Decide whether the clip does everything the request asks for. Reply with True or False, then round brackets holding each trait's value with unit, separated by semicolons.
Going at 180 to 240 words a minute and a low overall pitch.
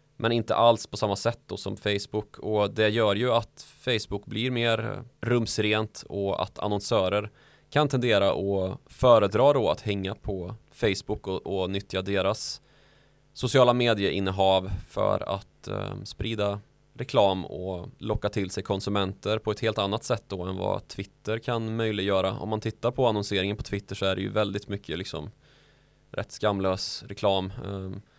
False (155 wpm; 105 Hz)